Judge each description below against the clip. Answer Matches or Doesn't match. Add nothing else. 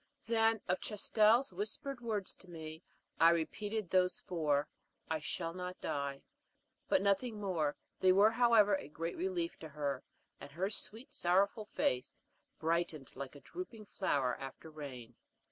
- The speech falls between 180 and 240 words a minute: Doesn't match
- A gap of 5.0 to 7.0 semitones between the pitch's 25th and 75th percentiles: Matches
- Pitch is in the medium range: Matches